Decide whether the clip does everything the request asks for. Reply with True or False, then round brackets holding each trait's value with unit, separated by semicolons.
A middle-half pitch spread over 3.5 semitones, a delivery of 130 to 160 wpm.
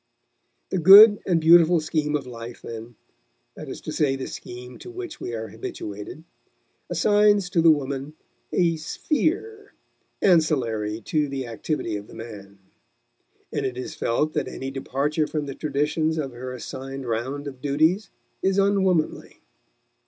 True (5.1 semitones; 150 wpm)